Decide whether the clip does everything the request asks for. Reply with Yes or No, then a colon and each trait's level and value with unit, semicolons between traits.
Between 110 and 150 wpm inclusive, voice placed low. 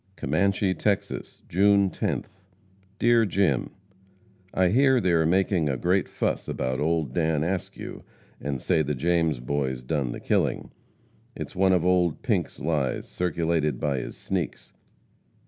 Yes: average, 140 wpm; very low, 85 Hz